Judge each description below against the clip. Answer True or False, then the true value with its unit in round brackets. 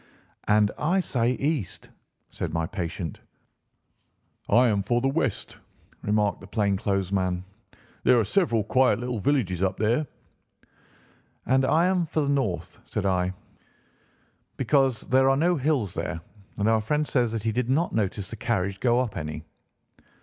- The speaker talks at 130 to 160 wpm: True (150 wpm)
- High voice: False (115 Hz)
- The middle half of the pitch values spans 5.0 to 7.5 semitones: True (5.3 semitones)